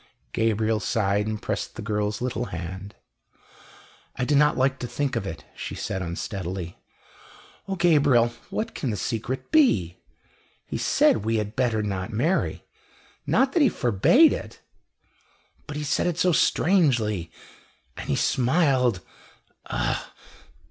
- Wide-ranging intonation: Yes, wide, 6.3 semitones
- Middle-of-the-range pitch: No, low, 115 Hz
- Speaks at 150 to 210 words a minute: No, average, 140 wpm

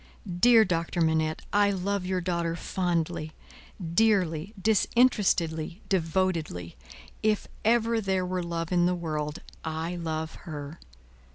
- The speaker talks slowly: Yes, slow, 115 wpm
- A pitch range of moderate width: Yes, average, 3.2 semitones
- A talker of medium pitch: Yes, medium, 175 Hz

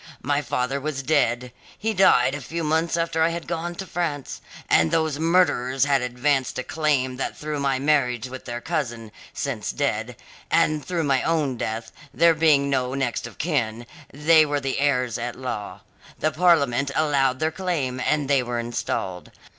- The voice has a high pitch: No, medium, 140 Hz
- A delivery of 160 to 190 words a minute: Yes, average, 175 wpm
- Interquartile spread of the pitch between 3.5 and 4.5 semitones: Yes, average, 3.9 semitones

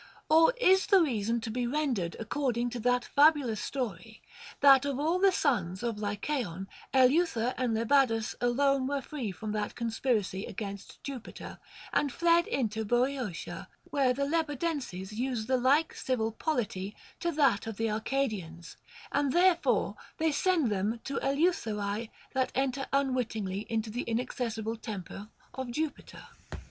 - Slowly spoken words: No, average, 145 wpm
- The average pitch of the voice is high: Yes, high, 245 Hz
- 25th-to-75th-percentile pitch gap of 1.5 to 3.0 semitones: No, average, 4.4 semitones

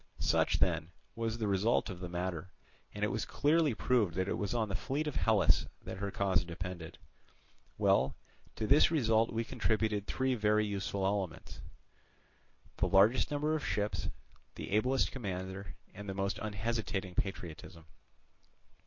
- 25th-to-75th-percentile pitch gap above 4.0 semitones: No, average, 3.6 semitones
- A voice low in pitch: Yes, low, 100 Hz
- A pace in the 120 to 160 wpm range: Yes, average, 155 wpm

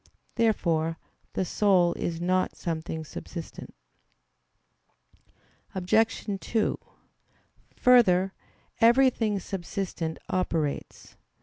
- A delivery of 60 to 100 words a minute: Yes, slow, 70 wpm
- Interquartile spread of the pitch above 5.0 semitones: No, average, 4.4 semitones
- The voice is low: No, medium, 185 Hz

